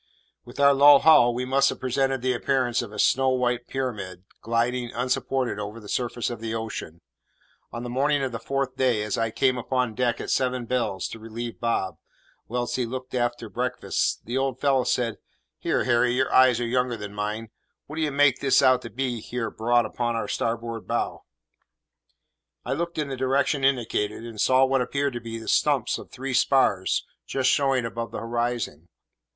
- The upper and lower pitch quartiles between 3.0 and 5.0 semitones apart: No, narrow, 2.4 semitones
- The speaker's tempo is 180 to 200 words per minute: Yes, average, 190 wpm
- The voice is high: No, low, 125 Hz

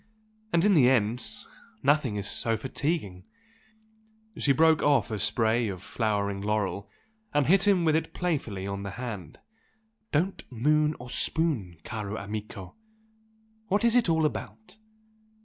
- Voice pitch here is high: No, low, 120 Hz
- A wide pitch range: Yes, wide, 7.4 semitones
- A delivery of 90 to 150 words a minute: Yes, average, 140 wpm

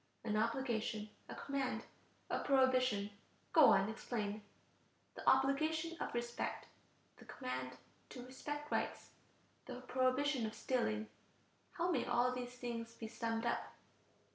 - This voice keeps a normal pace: No, slow, 125 wpm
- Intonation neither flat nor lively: Yes, average, 3.2 semitones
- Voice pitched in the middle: No, high, 245 Hz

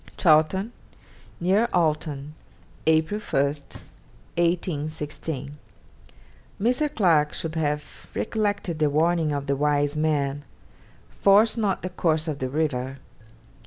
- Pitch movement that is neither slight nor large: Yes, average, 3.7 semitones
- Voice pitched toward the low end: No, medium, 155 Hz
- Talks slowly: Yes, slow, 105 wpm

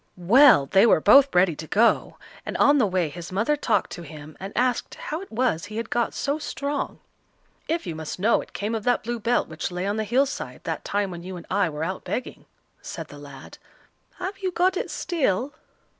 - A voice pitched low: No, high, 215 Hz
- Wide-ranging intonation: Yes, wide, 7.4 semitones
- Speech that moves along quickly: Yes, fast, 220 wpm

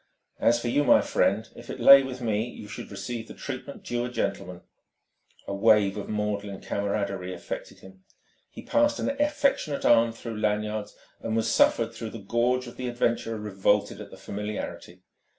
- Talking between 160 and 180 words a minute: Yes, average, 175 wpm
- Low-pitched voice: Yes, low, 110 Hz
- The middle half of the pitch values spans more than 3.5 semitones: No, average, 2.9 semitones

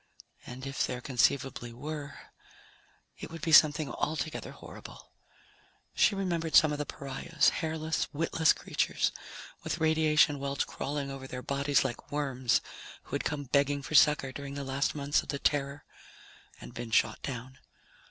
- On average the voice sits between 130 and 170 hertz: Yes, medium, 140 Hz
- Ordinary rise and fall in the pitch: No, narrow, 2.3 semitones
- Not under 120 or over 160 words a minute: Yes, average, 150 wpm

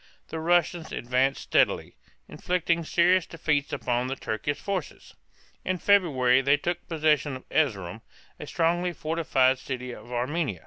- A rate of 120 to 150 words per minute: Yes, slow, 135 wpm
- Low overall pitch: No, medium, 145 Hz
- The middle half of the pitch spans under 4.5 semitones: No, average, 4.9 semitones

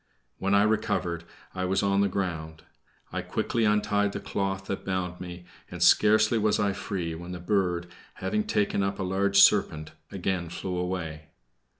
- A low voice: Yes, very low, 95 Hz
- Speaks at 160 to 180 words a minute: Yes, average, 170 wpm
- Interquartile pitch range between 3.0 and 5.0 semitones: No, narrow, 2.4 semitones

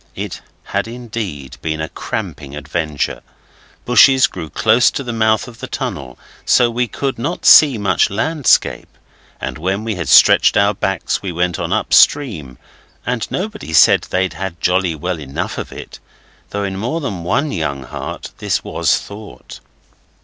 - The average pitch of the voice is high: No, low, 100 Hz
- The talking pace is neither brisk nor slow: Yes, average, 160 wpm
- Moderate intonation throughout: No, wide, 6.7 semitones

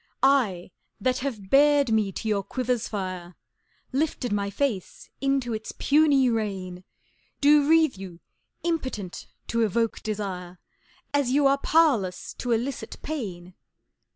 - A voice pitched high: Yes, high, 235 Hz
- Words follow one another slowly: Yes, slow, 125 wpm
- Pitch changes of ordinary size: No, wide, 6.0 semitones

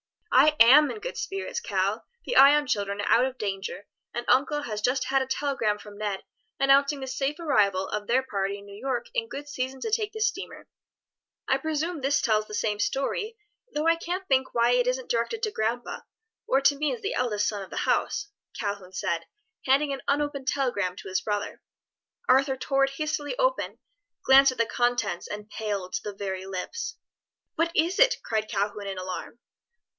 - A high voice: Yes, very high, 260 Hz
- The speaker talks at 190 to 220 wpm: Yes, average, 195 wpm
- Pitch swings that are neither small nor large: No, wide, 6.0 semitones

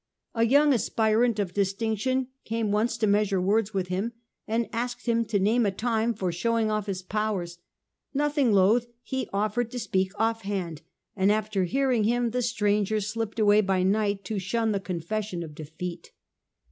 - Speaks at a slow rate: No, average, 170 wpm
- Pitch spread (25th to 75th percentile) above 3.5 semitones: No, average, 3.0 semitones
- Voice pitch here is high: Yes, high, 215 Hz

